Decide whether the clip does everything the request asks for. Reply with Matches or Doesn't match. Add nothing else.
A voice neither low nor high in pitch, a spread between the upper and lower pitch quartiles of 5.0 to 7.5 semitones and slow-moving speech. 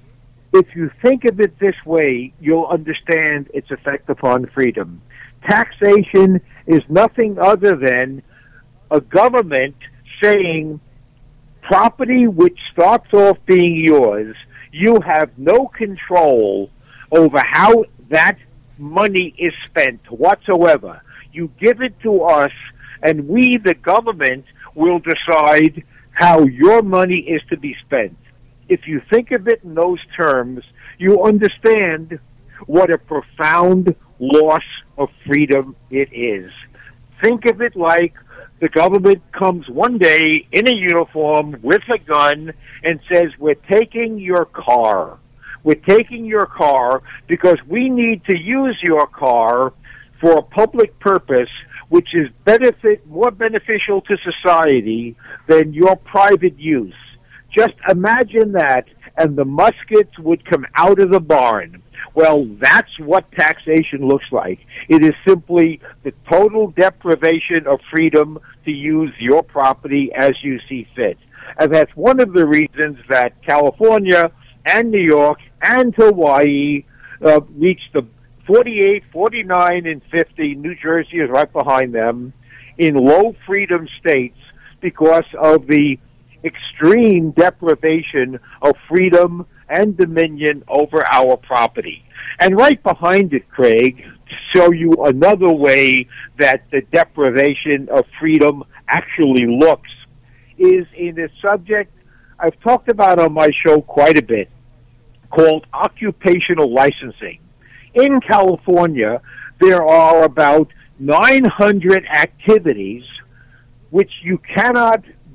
Matches